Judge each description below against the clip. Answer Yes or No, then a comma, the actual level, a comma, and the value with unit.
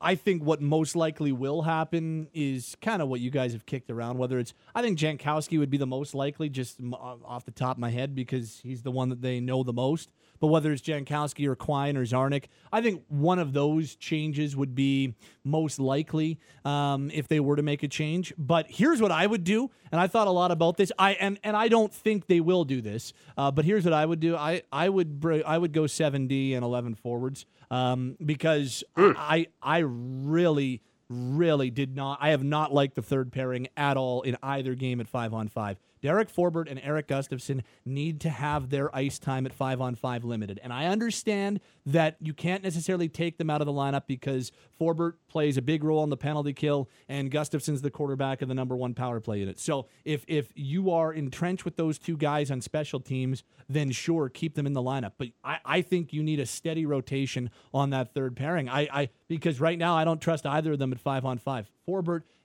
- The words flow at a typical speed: No, fast, 225 wpm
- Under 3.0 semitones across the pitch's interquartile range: No, average, 3.7 semitones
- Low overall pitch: No, medium, 145 Hz